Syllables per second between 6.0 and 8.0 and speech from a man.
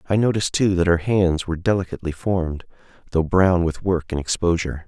Yes: 6.2 syllables/s; male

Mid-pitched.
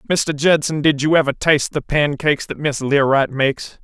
Yes: medium, 145 Hz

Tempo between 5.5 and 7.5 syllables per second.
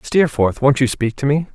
No: 5.0 syllables/s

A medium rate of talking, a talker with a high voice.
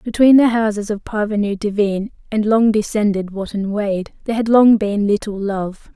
Yes: average, 170 wpm; high, 210 Hz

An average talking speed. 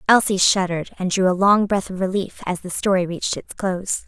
No: fast, 220 wpm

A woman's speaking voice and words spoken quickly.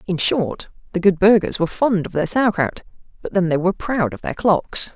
Yes: female; fast, 230 wpm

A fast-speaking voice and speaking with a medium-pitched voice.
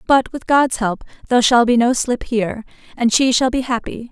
No: fast, 220 wpm; high, 240 Hz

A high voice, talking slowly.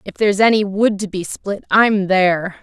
No: high, 200 Hz; fast, 205 wpm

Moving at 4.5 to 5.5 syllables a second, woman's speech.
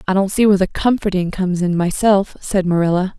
No: 6.0 syllables/s; female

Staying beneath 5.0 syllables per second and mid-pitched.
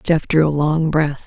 Yes: 4.1 syllables/s; medium, 155 Hz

